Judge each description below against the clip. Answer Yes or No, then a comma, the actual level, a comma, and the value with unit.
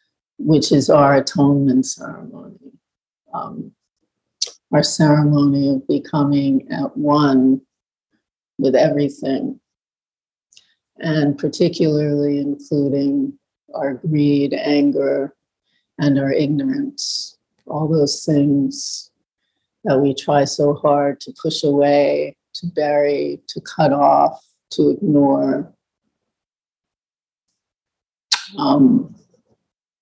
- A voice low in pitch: No, medium, 145 Hz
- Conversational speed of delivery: No, slow, 85 wpm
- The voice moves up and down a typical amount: No, narrow, 1.4 semitones